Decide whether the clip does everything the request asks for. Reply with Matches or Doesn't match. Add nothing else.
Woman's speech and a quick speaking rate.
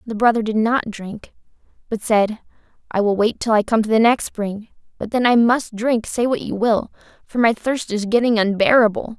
Matches